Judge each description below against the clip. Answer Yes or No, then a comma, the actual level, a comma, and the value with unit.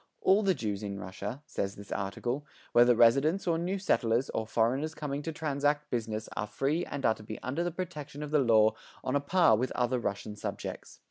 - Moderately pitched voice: No, low, 130 Hz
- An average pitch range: No, wide, 5.7 semitones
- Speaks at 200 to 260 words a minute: Yes, fast, 205 wpm